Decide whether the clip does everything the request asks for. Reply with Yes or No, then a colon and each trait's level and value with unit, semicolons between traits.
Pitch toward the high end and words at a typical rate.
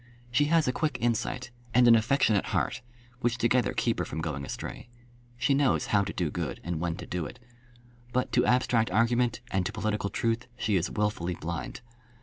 No: low, 115 Hz; average, 190 wpm